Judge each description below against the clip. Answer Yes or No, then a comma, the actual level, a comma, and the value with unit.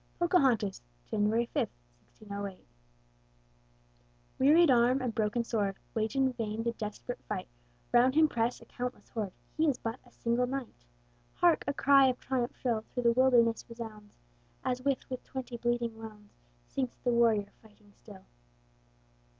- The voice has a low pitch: No, high, 235 Hz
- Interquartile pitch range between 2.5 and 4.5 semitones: Yes, average, 2.9 semitones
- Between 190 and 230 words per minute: No, average, 145 wpm